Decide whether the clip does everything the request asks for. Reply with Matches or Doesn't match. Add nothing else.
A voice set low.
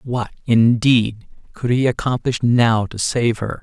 Matches